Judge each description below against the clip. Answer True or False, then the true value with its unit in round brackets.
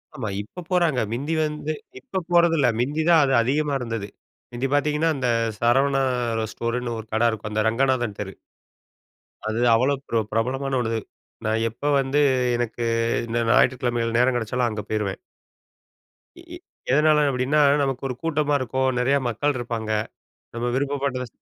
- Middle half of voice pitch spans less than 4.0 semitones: True (3.6 semitones)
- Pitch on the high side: False (130 Hz)